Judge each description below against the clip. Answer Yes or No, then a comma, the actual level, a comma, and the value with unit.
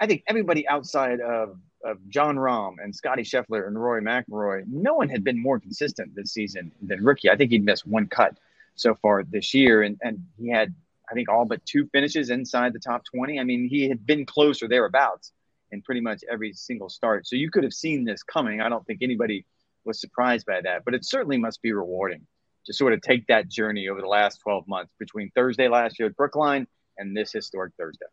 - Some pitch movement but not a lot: Yes, average, 4.2 semitones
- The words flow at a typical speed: No, fast, 220 wpm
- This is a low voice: Yes, low, 120 Hz